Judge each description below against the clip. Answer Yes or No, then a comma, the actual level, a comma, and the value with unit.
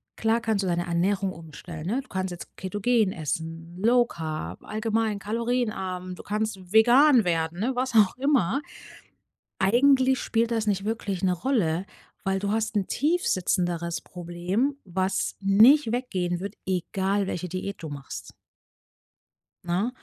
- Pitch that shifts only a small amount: No, average, 4.5 semitones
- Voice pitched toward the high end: Yes, high, 195 Hz